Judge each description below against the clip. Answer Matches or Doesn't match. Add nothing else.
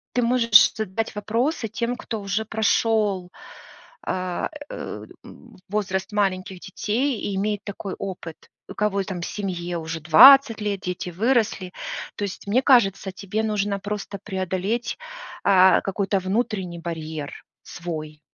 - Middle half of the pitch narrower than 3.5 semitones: Matches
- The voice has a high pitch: Matches